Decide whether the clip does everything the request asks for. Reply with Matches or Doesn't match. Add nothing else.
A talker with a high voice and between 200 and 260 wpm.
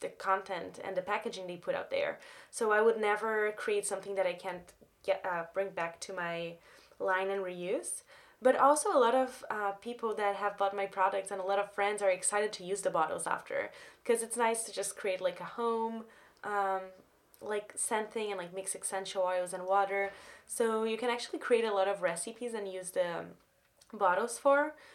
Matches